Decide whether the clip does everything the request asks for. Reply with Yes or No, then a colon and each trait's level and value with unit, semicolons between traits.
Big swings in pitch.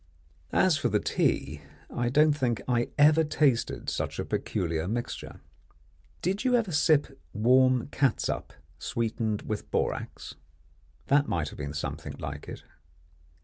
Yes: wide, 5.8 semitones